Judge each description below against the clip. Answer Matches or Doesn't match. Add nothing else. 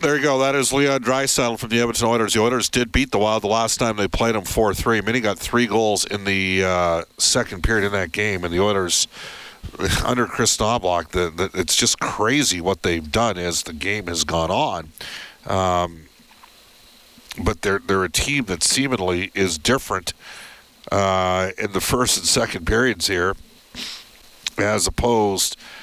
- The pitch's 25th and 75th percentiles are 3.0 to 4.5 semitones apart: Matches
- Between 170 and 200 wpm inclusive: Matches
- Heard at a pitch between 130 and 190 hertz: Doesn't match